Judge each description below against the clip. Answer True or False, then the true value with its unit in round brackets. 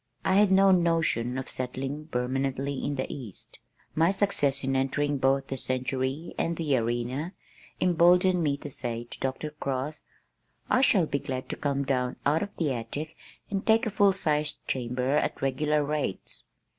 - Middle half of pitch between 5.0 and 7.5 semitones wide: False (4.0 semitones)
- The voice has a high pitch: False (140 Hz)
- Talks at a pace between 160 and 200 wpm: True (170 wpm)